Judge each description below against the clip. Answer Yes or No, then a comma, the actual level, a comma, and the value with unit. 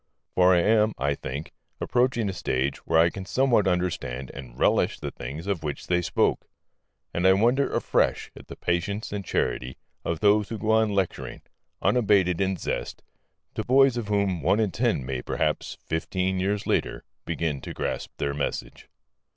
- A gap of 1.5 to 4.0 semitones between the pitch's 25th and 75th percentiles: No, average, 4.7 semitones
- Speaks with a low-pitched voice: Yes, very low, 95 Hz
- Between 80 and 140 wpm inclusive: No, average, 175 wpm